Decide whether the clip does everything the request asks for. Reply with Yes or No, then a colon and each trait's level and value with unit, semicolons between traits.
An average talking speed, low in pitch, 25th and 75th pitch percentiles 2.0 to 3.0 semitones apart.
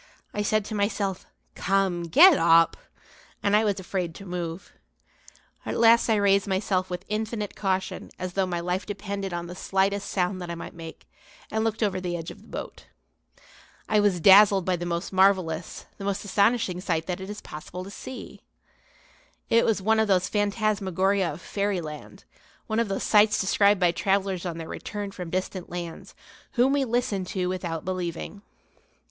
No: average, 175 wpm; high, 195 Hz; narrow, 2.6 semitones